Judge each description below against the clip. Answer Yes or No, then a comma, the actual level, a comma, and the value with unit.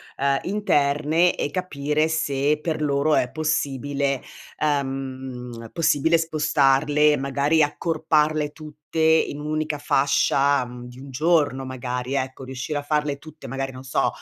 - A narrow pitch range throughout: Yes, narrow, 2.3 semitones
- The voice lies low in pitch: No, medium, 145 Hz